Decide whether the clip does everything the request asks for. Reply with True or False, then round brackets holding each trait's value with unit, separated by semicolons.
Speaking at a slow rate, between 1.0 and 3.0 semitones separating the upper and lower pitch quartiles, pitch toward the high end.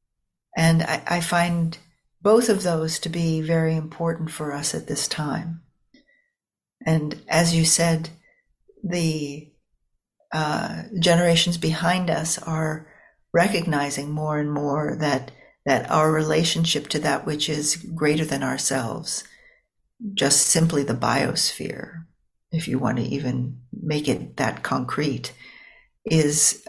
False (125 wpm; 2.4 semitones; 160 Hz)